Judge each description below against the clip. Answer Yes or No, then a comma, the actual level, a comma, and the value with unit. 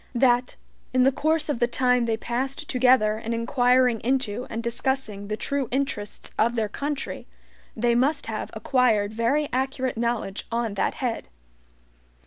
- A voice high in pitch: Yes, high, 245 Hz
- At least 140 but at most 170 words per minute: Yes, average, 150 wpm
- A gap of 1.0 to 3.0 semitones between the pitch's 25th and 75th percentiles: Yes, narrow, 2.6 semitones